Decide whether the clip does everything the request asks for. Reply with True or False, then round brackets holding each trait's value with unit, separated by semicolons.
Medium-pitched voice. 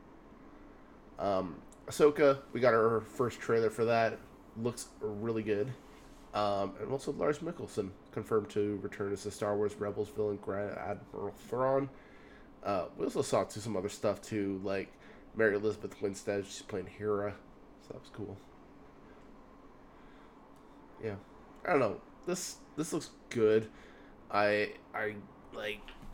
False (105 Hz)